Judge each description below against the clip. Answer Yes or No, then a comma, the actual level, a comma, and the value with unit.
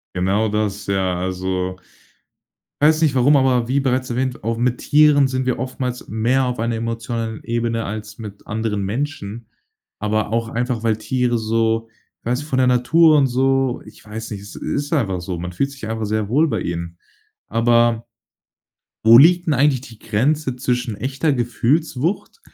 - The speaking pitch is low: Yes, low, 120 Hz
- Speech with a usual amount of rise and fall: Yes, average, 3.5 semitones